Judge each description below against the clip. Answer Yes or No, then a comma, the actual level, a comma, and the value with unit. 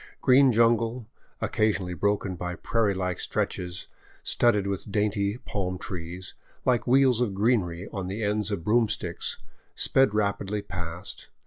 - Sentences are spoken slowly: Yes, slow, 130 wpm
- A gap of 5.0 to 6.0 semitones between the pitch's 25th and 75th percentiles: No, average, 3.7 semitones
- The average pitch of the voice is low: Yes, low, 100 Hz